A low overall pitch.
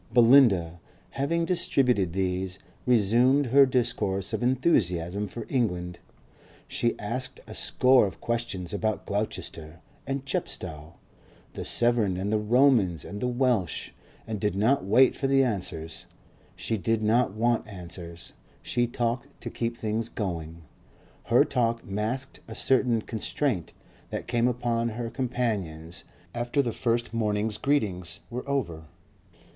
Yes: low, 115 Hz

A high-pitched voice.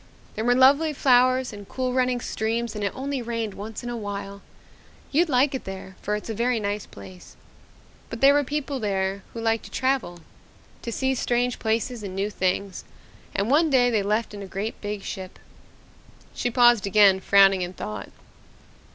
Yes: high, 225 Hz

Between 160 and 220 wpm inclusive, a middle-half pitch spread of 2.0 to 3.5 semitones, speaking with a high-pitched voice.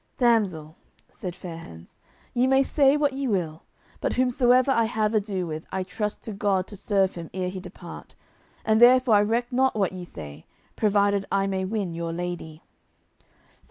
No: average, 175 wpm; average, 5.0 semitones; high, 200 Hz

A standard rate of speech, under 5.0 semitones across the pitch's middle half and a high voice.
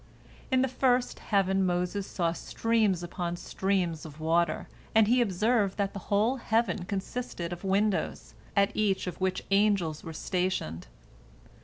Yes: average, 145 wpm; average, 3.4 semitones; high, 195 Hz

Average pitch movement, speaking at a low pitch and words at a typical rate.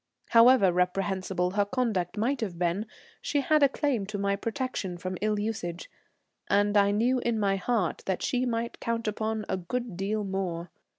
No: average, 3.6 semitones; high, 205 Hz; average, 175 wpm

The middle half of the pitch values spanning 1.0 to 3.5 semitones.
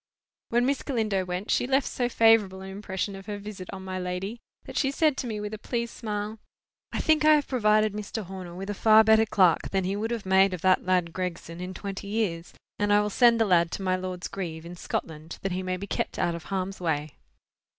Yes: average, 3.2 semitones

